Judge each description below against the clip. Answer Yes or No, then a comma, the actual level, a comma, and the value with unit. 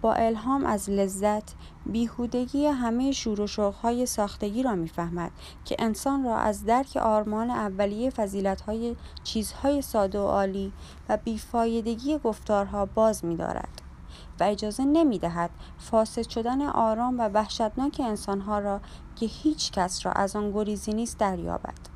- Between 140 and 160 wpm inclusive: No, average, 130 wpm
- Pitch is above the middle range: Yes, high, 220 Hz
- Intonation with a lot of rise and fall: No, average, 2.9 semitones